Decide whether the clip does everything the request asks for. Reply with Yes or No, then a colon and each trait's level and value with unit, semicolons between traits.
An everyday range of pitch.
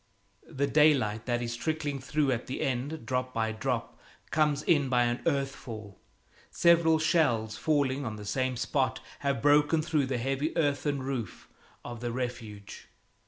Yes: average, 3.7 semitones